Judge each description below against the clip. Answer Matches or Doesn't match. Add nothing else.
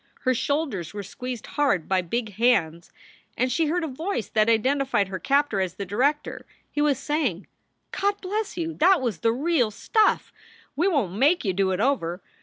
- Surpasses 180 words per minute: Matches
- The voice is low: Doesn't match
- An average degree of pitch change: Doesn't match